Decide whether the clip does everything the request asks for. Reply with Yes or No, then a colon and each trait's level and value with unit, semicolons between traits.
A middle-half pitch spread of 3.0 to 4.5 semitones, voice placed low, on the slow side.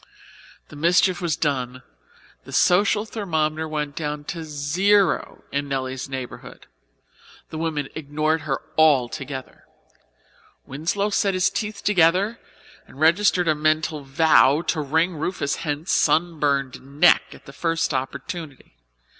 No: average, 3.6 semitones; medium, 155 Hz; slow, 120 wpm